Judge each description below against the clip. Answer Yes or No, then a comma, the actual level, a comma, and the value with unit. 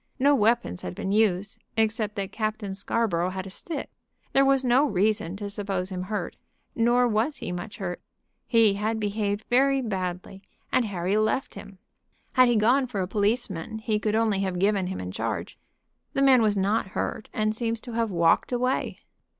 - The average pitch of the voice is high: Yes, high, 210 Hz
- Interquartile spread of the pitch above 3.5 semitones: No, average, 3.2 semitones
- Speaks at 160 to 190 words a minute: Yes, average, 185 wpm